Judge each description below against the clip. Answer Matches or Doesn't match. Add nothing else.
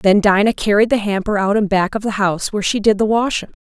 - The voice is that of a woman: Matches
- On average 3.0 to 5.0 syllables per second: Doesn't match